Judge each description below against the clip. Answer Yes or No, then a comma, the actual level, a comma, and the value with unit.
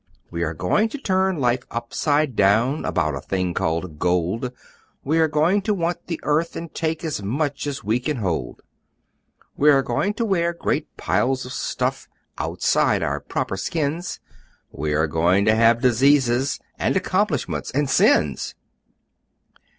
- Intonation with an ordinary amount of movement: No, wide, 8.5 semitones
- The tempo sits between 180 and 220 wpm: No, average, 155 wpm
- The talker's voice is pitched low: Yes, low, 130 Hz